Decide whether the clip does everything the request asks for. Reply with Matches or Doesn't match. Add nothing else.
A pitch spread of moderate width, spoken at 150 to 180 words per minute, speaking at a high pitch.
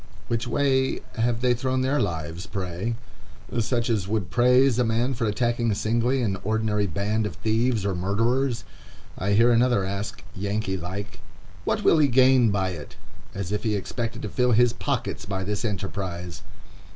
Doesn't match